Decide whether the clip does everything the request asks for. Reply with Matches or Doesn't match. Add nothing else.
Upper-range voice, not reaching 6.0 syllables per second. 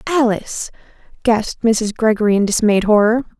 Matches